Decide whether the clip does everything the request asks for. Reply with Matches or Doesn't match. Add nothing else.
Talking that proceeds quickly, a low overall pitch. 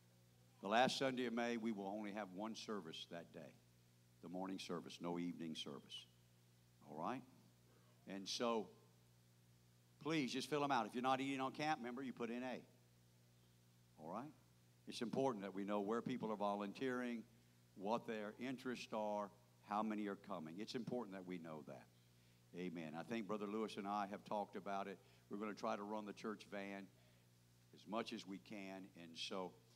Doesn't match